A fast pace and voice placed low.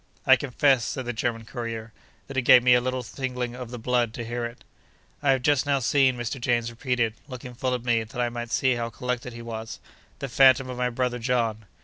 Yes: fast, 230 wpm; low, 125 Hz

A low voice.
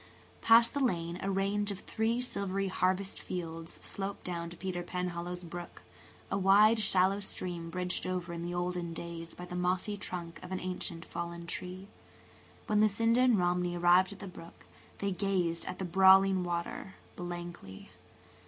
No: medium, 180 Hz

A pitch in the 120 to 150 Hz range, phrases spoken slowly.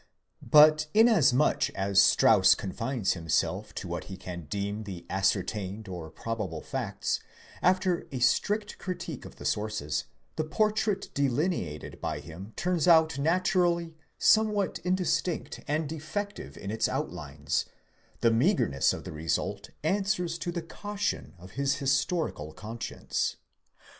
Yes: medium, 140 Hz; slow, 130 wpm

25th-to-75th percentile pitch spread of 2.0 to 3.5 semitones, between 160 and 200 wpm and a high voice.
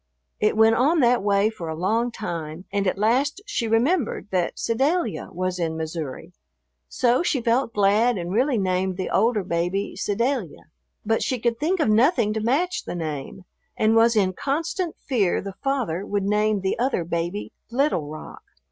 No: average, 5.1 semitones; average, 175 wpm; high, 215 Hz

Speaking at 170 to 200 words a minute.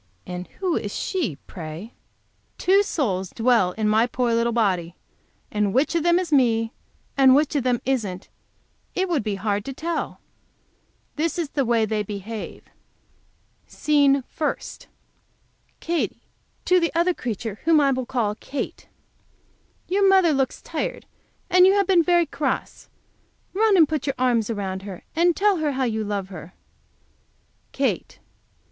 No: average, 155 wpm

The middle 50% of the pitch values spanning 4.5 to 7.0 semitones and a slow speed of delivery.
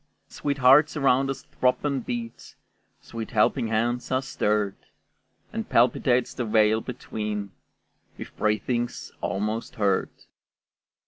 No: average, 3.2 semitones; slow, 115 wpm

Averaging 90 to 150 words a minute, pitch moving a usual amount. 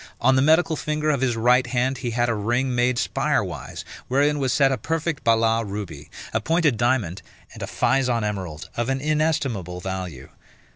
No: average, 185 wpm; average, 4.0 semitones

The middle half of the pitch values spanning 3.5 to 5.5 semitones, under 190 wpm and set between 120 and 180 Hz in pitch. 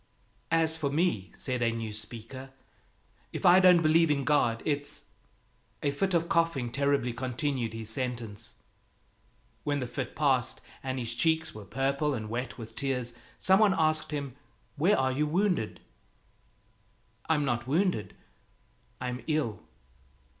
Yes: average, 4.7 semitones; average, 145 wpm; low, 135 Hz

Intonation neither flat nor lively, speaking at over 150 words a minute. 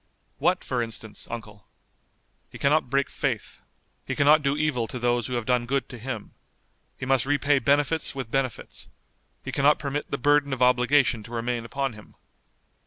Yes: average, 3.0 semitones; average, 175 wpm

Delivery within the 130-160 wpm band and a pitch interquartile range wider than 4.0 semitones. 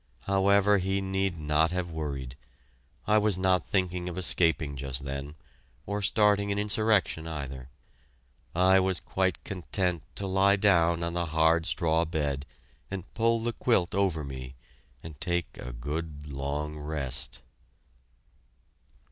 Yes: slow, 135 wpm; average, 4.5 semitones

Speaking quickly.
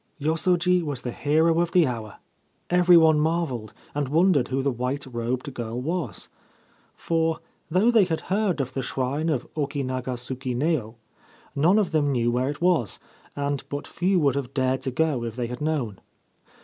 No: average, 180 wpm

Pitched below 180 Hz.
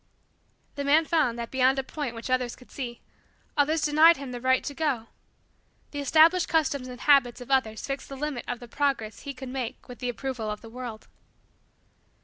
No: very high, 265 Hz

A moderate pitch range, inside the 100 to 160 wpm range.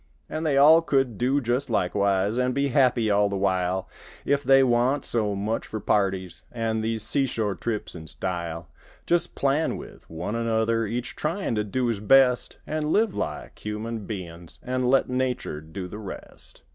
No: average, 5.0 semitones; average, 170 wpm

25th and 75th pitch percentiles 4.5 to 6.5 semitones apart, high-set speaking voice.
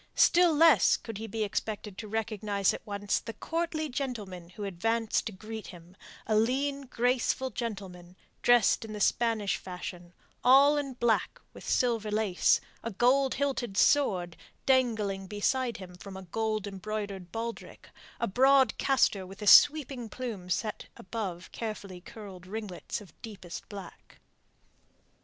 No: average, 4.1 semitones; high, 215 Hz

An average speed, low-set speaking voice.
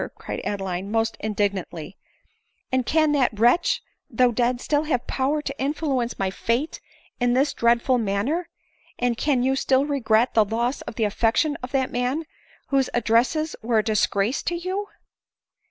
No: average, 160 wpm; high, 245 Hz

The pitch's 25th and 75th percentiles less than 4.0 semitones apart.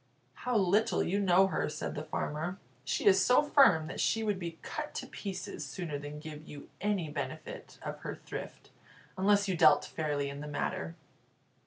No: average, 5.0 semitones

